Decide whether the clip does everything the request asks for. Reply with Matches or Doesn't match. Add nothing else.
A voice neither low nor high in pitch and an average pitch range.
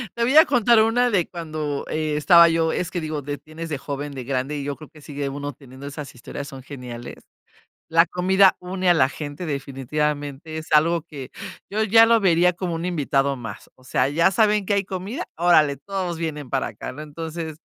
Matches